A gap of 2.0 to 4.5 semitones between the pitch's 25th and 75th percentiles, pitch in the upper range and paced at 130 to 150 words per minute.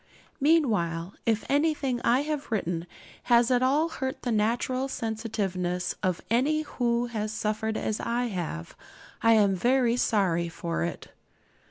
No: average, 5.0 semitones; high, 230 Hz; average, 140 wpm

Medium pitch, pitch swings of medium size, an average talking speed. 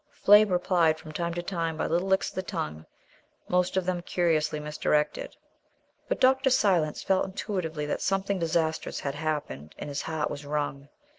Yes: medium, 165 Hz; average, 3.8 semitones; average, 170 wpm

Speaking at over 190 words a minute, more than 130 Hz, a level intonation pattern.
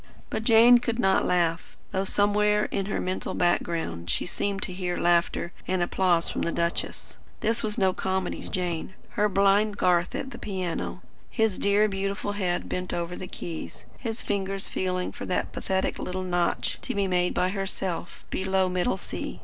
No: average, 175 wpm; high, 190 Hz; narrow, 2.3 semitones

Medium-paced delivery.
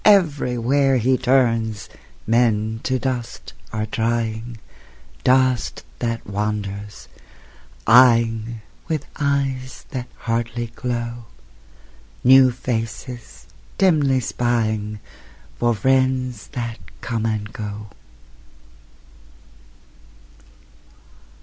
No: slow, 75 wpm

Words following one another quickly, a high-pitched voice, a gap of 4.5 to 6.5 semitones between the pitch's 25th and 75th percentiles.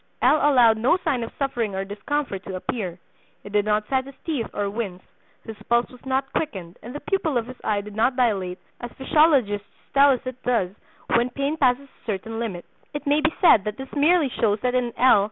Yes: fast, 215 wpm; high, 240 Hz; average, 4.9 semitones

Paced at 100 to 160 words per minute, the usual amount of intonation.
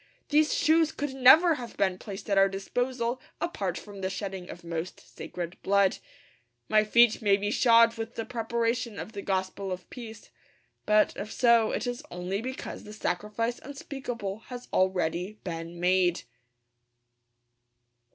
Yes: average, 150 wpm; average, 4.1 semitones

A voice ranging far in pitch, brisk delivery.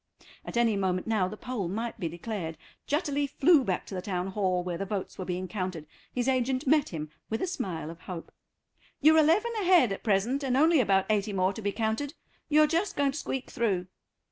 Yes: wide, 7.0 semitones; fast, 210 wpm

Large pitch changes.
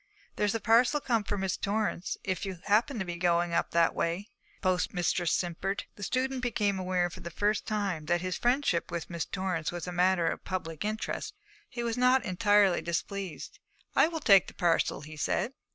No: average, 3.7 semitones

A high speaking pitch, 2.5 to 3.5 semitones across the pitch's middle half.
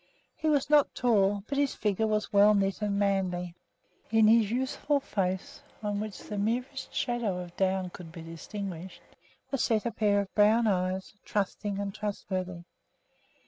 Yes: high, 205 Hz; average, 2.8 semitones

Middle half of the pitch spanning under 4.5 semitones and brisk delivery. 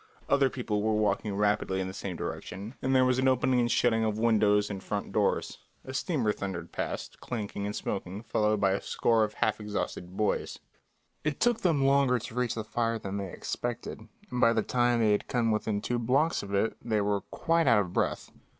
Yes: average, 3.3 semitones; fast, 210 wpm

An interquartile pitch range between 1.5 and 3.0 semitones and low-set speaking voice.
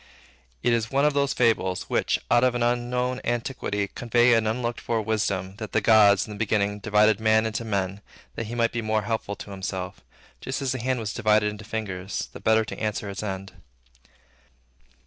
Yes: narrow, 2.6 semitones; low, 110 Hz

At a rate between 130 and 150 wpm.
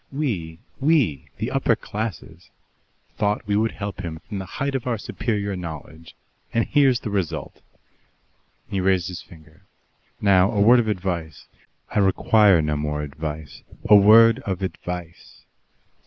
Yes: average, 145 wpm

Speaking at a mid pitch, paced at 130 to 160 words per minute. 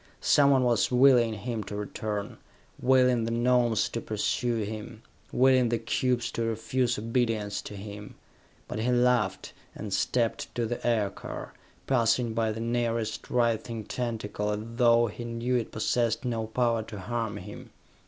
No: low, 115 Hz; average, 150 wpm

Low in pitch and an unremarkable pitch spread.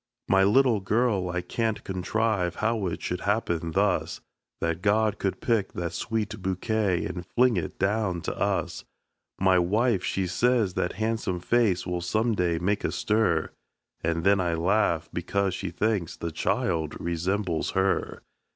Yes: very low, 95 Hz; average, 3.7 semitones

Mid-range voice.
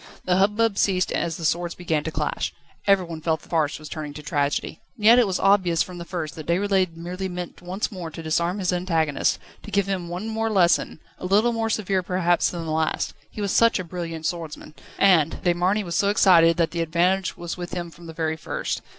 Yes: medium, 175 Hz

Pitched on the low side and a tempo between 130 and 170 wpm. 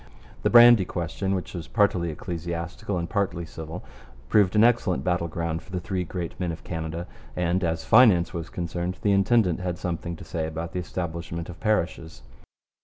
No: very low, 90 Hz; average, 180 wpm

